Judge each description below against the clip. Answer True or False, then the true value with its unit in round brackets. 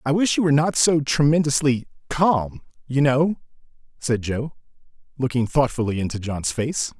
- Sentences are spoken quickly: False (145 wpm)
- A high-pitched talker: False (135 Hz)